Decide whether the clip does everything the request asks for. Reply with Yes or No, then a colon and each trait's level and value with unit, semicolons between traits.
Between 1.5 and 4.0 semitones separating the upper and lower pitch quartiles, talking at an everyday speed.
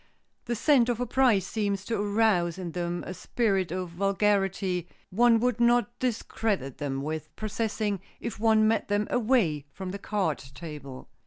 No: average, 4.4 semitones; average, 160 wpm